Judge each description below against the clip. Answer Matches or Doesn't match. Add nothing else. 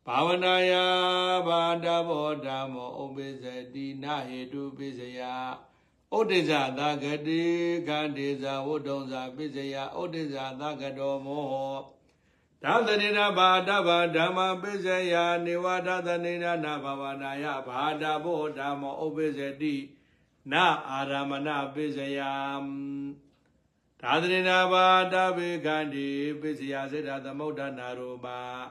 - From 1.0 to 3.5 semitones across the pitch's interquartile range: Doesn't match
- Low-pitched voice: Doesn't match